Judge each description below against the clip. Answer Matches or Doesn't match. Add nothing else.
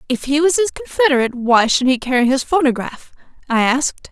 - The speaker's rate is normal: Matches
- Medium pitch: Doesn't match